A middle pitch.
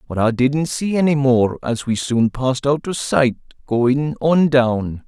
No: low, 130 Hz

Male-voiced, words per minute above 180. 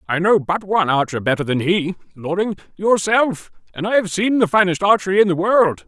Yes: male; average, 195 wpm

